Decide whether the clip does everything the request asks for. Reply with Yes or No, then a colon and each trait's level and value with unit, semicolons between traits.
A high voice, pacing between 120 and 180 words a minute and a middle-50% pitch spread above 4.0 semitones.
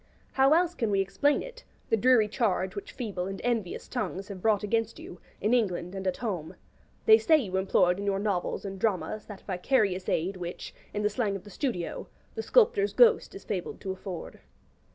No: high, 205 Hz; average, 195 wpm; average, 4.7 semitones